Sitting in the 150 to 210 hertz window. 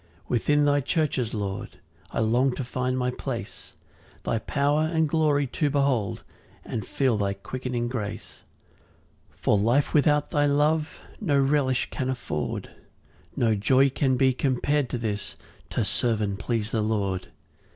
No: low, 130 Hz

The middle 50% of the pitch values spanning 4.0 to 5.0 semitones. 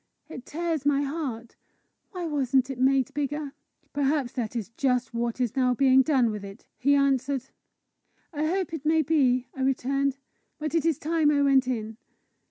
No: average, 2.8 semitones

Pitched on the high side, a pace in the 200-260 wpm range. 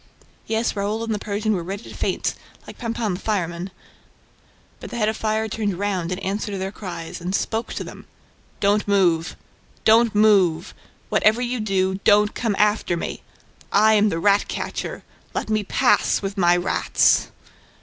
No: high, 205 Hz; average, 170 wpm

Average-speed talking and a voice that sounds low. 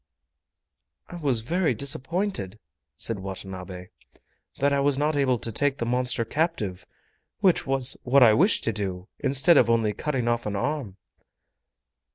Yes: average, 145 wpm; low, 125 Hz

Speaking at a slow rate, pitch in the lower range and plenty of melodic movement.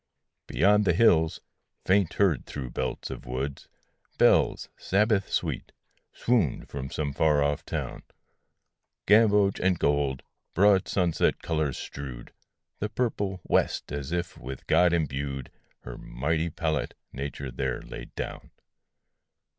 Yes: slow, 125 wpm; very low, 80 Hz; wide, 5.8 semitones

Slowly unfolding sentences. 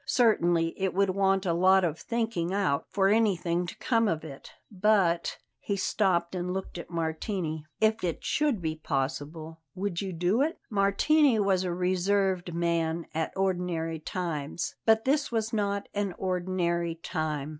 No: average, 155 wpm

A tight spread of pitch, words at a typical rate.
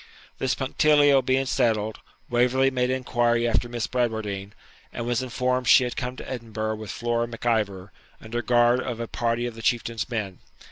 Yes: narrow, 2.2 semitones; average, 175 wpm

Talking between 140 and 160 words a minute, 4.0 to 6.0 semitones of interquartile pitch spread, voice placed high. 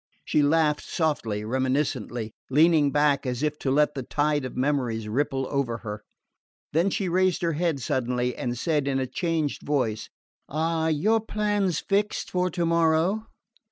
No: average, 155 wpm; average, 4.3 semitones; medium, 150 Hz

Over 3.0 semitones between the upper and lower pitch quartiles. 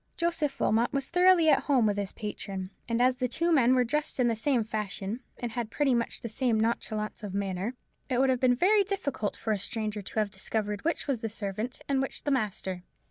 Yes: average, 4.3 semitones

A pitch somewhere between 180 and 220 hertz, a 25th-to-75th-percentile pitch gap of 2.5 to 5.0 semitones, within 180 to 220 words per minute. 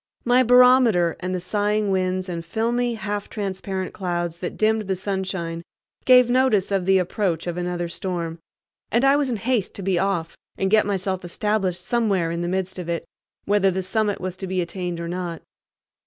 Yes: high, 190 Hz; average, 3.3 semitones; average, 185 wpm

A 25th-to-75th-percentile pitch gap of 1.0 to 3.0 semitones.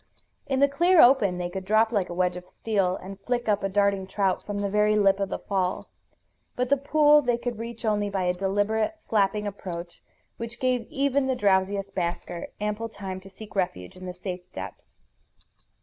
No: average, 3.6 semitones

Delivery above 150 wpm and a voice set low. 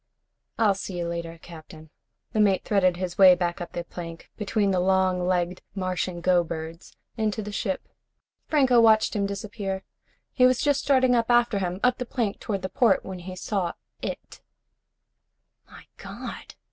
No: average, 165 wpm; high, 190 Hz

